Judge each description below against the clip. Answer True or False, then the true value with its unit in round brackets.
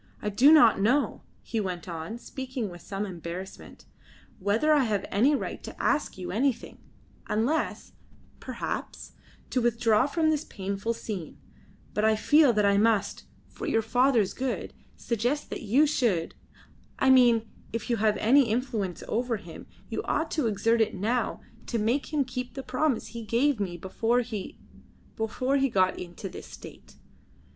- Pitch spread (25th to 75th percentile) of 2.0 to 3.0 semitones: False (4.4 semitones)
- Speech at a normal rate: True (160 wpm)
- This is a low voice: False (230 Hz)